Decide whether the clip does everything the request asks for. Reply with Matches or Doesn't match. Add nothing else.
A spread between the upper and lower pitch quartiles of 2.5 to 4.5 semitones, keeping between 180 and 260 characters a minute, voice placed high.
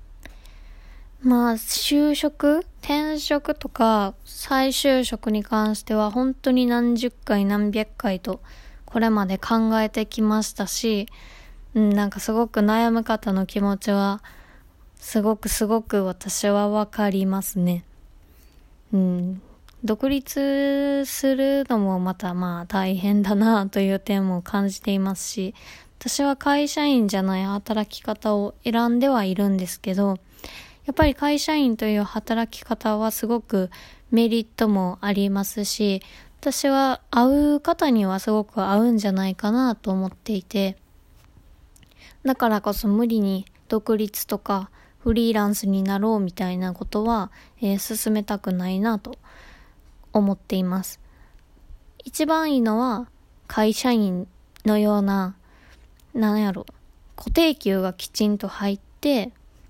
Matches